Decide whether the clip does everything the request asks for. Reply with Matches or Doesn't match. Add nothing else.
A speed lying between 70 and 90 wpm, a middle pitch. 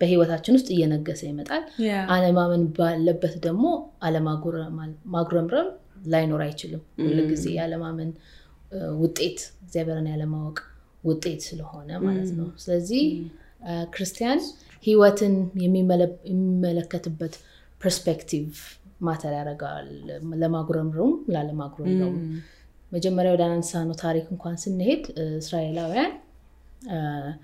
Matches